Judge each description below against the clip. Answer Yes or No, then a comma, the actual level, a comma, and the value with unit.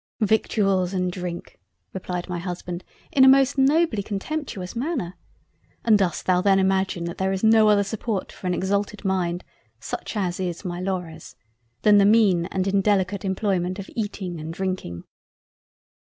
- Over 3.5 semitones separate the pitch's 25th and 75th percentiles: No, average, 2.7 semitones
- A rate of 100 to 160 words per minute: Yes, average, 155 wpm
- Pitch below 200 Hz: Yes, high, 190 Hz